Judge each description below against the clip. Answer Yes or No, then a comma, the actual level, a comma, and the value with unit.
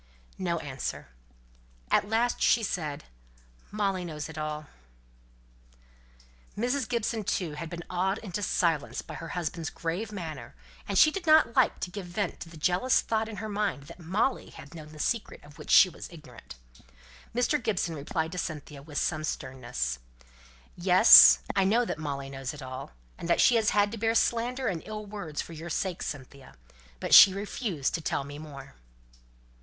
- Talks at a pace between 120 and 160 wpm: No, average, 175 wpm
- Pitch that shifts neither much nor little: No, wide, 5.8 semitones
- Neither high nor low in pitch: Yes, medium, 175 Hz